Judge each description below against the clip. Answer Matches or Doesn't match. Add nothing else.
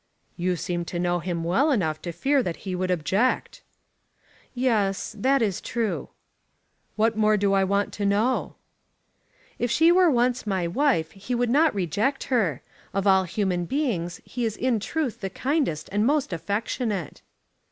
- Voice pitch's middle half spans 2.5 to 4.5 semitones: Doesn't match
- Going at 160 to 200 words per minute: Matches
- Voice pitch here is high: Matches